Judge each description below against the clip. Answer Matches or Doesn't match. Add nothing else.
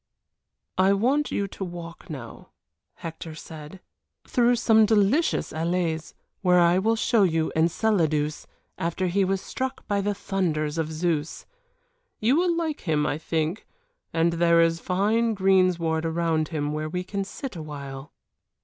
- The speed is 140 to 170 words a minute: Matches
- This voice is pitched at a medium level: Matches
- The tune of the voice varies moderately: Matches